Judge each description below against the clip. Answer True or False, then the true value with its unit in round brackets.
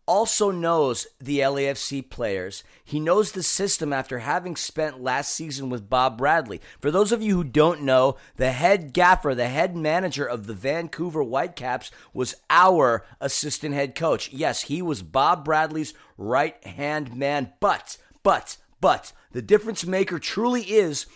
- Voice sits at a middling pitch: True (150 Hz)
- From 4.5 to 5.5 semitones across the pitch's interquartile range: True (4.9 semitones)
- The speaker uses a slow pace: False (155 wpm)